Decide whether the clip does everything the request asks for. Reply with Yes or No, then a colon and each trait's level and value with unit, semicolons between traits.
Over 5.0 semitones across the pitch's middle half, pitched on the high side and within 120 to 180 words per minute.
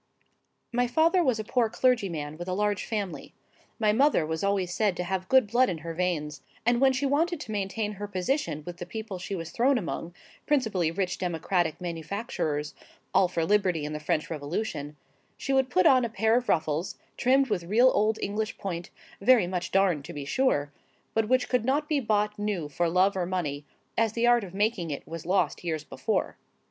No: wide, 5.6 semitones; high, 195 Hz; average, 195 wpm